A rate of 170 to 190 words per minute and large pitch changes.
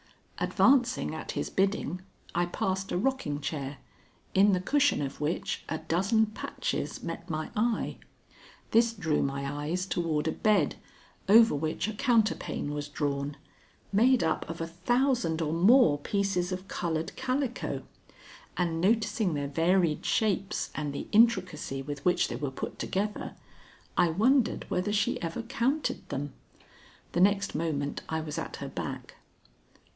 No: average, 145 wpm; wide, 5.7 semitones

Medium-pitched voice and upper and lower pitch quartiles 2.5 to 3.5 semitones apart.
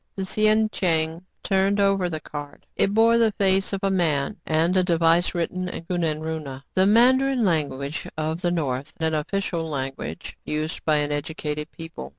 No: medium, 165 Hz; average, 4.0 semitones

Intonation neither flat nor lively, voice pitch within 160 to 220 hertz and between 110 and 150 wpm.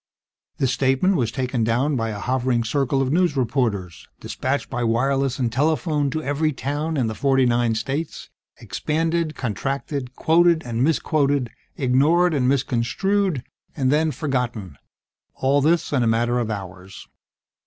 No: average, 4.0 semitones; low, 135 Hz; average, 145 wpm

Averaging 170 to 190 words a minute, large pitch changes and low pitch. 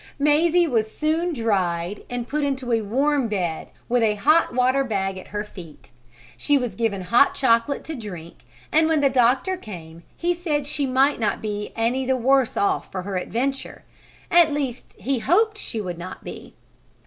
No: average, 180 wpm; wide, 5.8 semitones; high, 245 Hz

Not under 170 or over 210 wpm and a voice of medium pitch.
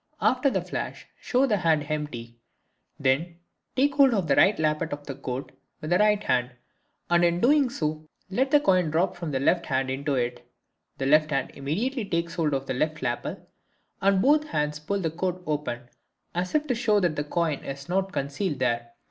Yes: average, 200 wpm; medium, 160 Hz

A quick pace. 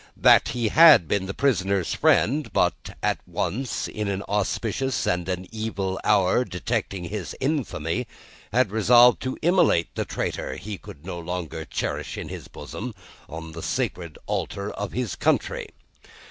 No: average, 150 wpm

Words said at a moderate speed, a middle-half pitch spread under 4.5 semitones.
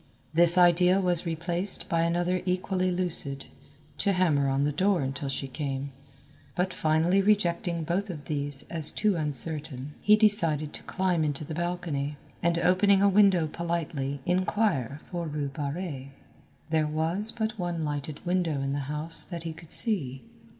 Yes: average, 155 wpm; average, 3.7 semitones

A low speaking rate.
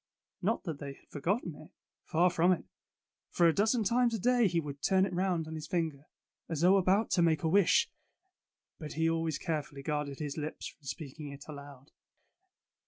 No: average, 190 wpm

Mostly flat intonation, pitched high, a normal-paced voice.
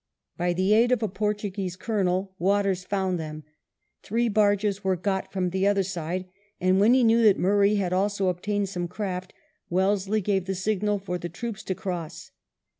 Yes: narrow, 2.2 semitones; high, 195 Hz; average, 180 wpm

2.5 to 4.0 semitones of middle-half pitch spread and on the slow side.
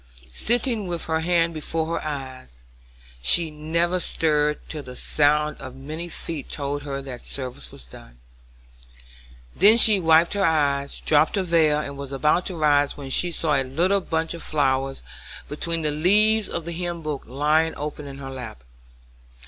No: average, 3.3 semitones; average, 170 wpm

